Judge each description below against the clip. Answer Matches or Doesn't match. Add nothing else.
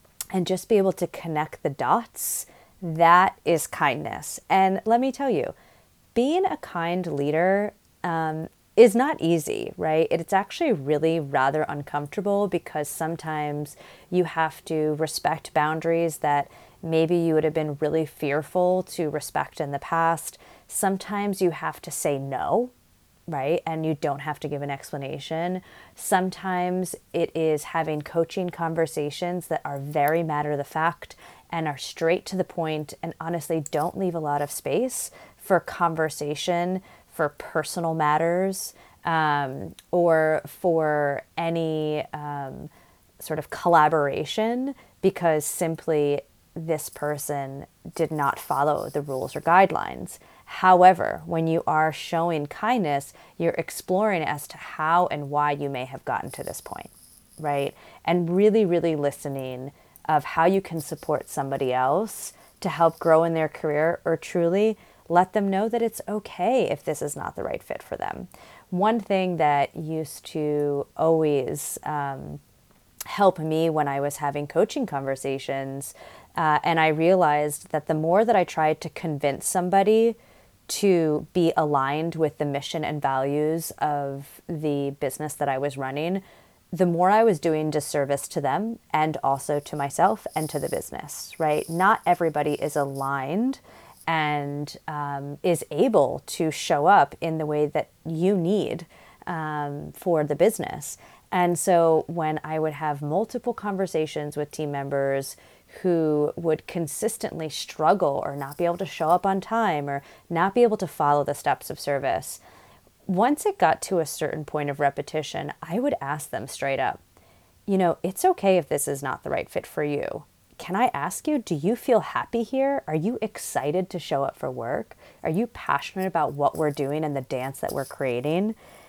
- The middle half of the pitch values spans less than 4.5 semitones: Matches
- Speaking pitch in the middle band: Matches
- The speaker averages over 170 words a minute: Doesn't match